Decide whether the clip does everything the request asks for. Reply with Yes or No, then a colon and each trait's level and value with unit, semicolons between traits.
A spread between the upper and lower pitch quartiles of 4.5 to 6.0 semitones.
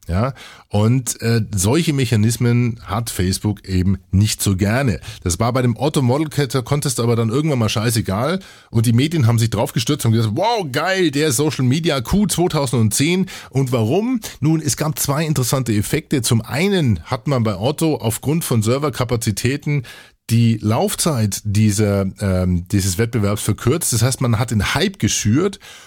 Yes: average, 5.0 semitones